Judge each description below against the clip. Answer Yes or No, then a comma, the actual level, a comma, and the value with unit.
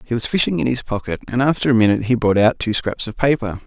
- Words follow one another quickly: Yes, fast, 280 wpm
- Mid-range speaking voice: No, low, 115 Hz